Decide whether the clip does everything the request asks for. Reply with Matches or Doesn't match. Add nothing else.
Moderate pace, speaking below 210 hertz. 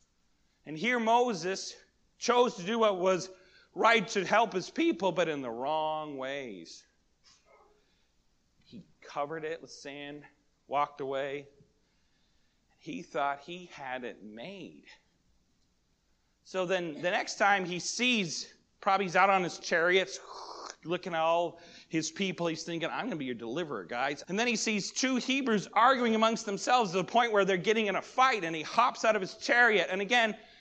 Matches